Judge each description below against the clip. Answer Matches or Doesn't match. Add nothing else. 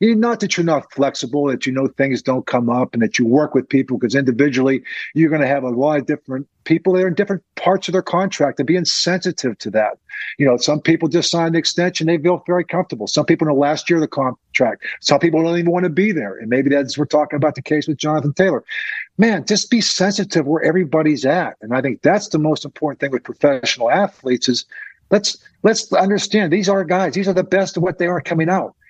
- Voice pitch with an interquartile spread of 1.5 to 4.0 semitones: Doesn't match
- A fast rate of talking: Matches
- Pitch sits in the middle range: Matches